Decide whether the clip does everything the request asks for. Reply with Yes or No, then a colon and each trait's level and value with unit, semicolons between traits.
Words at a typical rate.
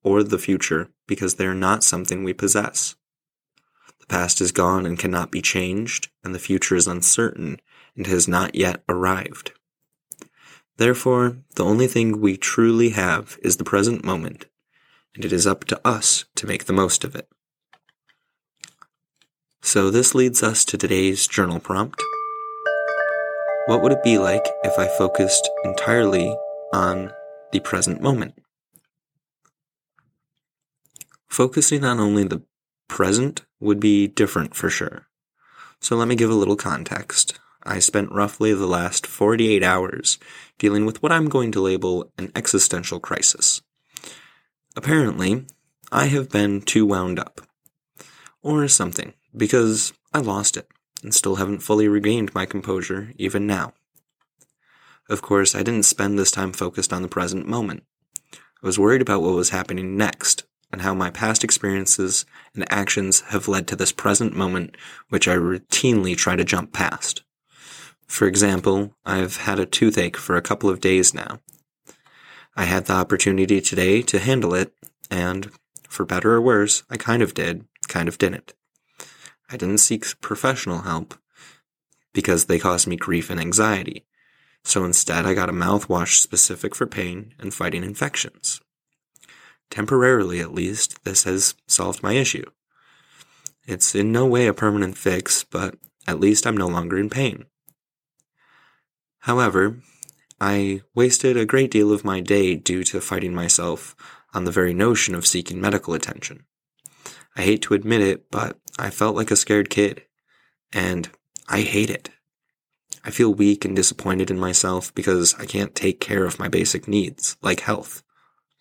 Yes: average, 150 wpm